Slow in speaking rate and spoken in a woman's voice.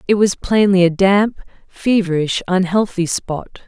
Yes: slow, 130 wpm; female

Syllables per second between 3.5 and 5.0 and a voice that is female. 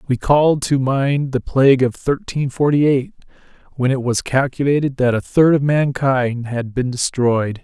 No: 4.5 syllables/s; male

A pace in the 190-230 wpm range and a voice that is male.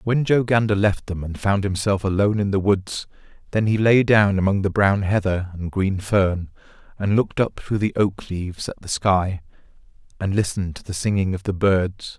Yes: average, 200 wpm; male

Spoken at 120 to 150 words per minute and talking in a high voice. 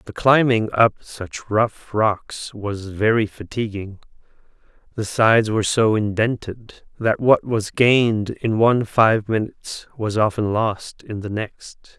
No: average, 140 wpm; low, 110 Hz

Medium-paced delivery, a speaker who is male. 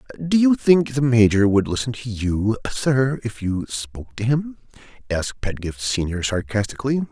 Yes: average, 160 wpm; male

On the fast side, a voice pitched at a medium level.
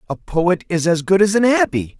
Yes: fast, 240 wpm; medium, 175 Hz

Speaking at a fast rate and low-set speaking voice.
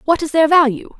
No: fast, 240 wpm; very high, 305 Hz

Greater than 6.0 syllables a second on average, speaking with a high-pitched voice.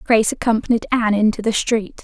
Yes: 6.5 syllables/s; high, 220 Hz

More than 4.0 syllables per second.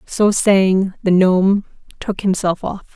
No: 3.8 syllables/s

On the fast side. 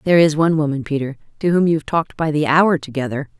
Yes: fast, 245 wpm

